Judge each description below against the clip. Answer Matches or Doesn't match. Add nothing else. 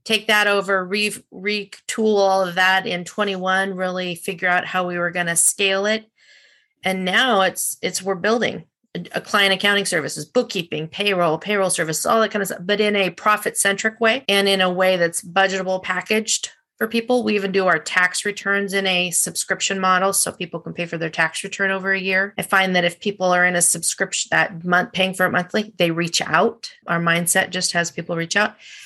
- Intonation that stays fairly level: Matches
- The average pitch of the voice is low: Doesn't match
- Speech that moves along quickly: Matches